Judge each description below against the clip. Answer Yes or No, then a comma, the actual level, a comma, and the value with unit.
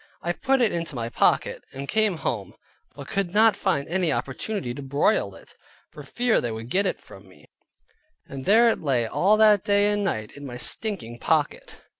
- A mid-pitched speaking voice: Yes, medium, 170 Hz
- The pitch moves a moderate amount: No, wide, 8.6 semitones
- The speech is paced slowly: No, average, 195 wpm